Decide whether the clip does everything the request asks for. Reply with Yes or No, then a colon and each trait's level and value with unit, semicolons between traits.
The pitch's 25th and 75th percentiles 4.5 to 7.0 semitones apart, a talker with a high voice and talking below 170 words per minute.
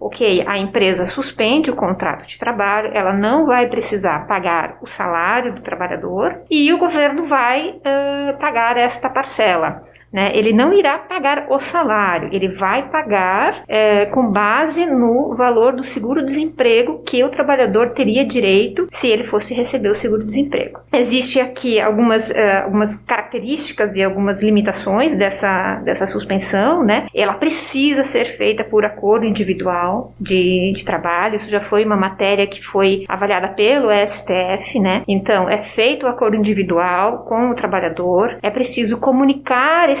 Yes: average, 5.2 semitones; high, 225 Hz; average, 150 wpm